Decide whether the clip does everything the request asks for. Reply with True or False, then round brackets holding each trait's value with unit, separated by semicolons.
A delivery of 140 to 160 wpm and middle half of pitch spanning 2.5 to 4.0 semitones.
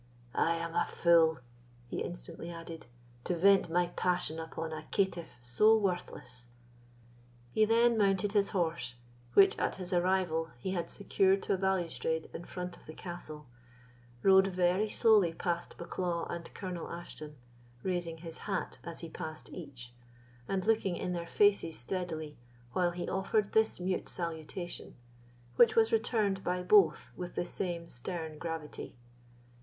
True (150 wpm; 2.8 semitones)